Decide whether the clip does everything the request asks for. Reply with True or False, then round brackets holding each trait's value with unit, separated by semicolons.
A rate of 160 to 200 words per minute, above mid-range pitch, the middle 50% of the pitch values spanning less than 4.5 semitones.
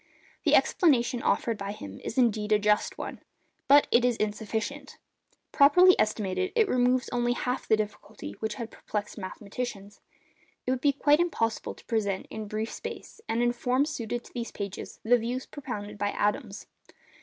True (165 wpm; 230 Hz; 3.4 semitones)